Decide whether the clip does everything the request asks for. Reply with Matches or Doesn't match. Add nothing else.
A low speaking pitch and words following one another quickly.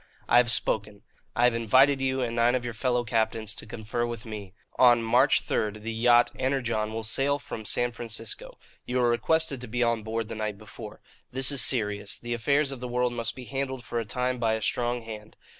Matches